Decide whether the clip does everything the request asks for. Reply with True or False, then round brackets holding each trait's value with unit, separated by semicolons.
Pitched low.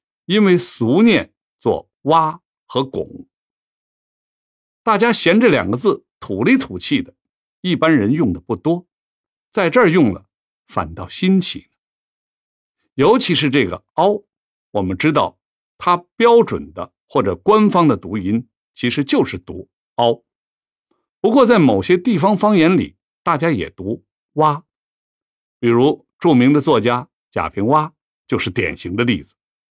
False (170 Hz)